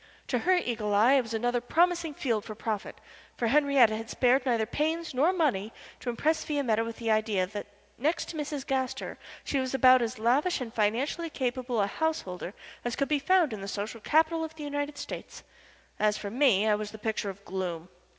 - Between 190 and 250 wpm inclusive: Yes, average, 200 wpm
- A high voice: Yes, high, 245 Hz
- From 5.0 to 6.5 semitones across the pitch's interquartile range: Yes, average, 5.3 semitones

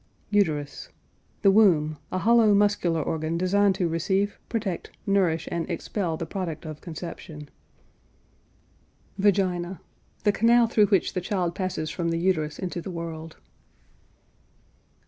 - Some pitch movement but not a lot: Yes, average, 3.6 semitones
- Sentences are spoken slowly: Yes, slow, 125 wpm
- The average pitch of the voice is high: No, medium, 180 Hz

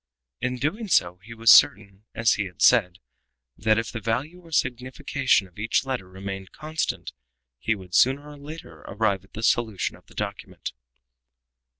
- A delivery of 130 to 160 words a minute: No, average, 170 wpm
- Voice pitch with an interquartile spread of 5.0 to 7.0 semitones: Yes, wide, 5.5 semitones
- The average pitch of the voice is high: No, low, 115 Hz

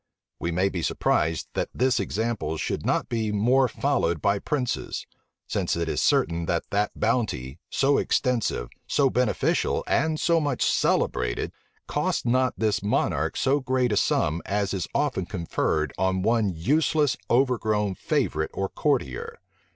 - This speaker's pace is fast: No, average, 145 wpm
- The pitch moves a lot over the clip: Yes, wide, 7.0 semitones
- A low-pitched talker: Yes, low, 105 Hz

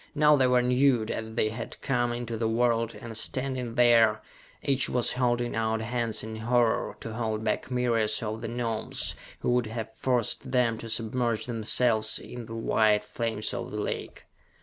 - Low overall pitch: Yes, low, 115 Hz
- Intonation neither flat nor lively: No, narrow, 1.8 semitones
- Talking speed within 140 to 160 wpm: No, average, 175 wpm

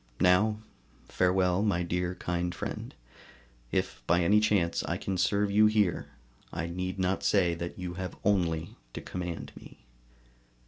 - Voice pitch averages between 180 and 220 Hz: No, very low, 90 Hz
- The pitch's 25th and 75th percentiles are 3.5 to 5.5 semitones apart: No, narrow, 2.4 semitones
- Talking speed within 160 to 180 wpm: No, average, 145 wpm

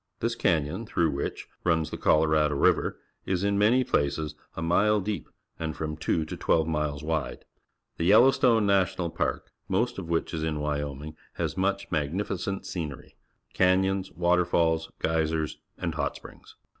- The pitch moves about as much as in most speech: Yes, average, 3.8 semitones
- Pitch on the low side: Yes, very low, 85 Hz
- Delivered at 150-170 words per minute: Yes, average, 160 wpm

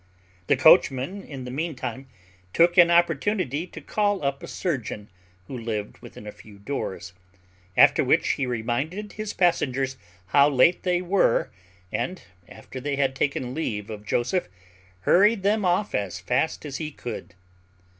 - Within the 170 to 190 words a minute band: No, average, 150 wpm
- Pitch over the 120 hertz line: Yes, medium, 140 Hz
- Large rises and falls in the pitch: Yes, wide, 6.3 semitones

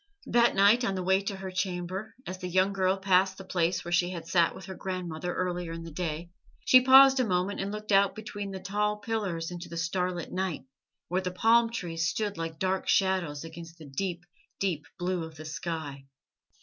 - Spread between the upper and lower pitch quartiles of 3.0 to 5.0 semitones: No, narrow, 2.6 semitones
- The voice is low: No, medium, 185 Hz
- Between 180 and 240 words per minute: Yes, fast, 205 wpm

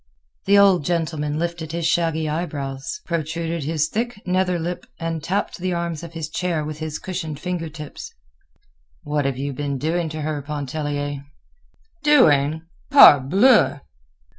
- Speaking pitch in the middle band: Yes, medium, 160 Hz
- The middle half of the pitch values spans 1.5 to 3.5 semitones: Yes, average, 2.8 semitones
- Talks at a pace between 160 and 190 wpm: No, average, 140 wpm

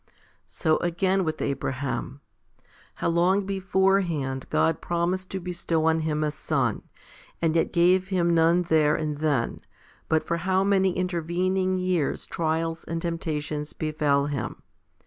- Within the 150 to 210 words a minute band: No, average, 140 wpm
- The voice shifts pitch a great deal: No, average, 3.0 semitones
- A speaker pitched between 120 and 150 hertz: No, medium, 170 Hz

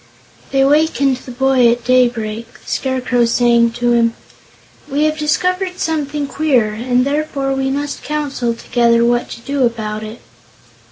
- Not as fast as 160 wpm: Yes, average, 150 wpm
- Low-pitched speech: No, very high, 255 Hz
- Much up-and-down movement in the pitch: No, average, 3.3 semitones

